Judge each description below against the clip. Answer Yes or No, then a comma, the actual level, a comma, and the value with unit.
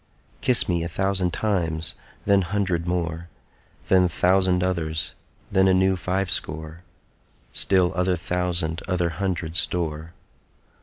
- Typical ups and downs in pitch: No, narrow, 2.1 semitones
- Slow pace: Yes, slow, 120 wpm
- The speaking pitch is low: Yes, very low, 90 Hz